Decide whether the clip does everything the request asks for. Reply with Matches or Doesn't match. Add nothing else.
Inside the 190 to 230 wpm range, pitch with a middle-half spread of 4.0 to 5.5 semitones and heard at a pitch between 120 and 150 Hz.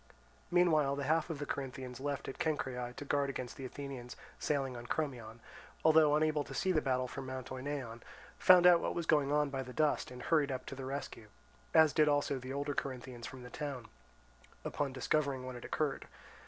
Doesn't match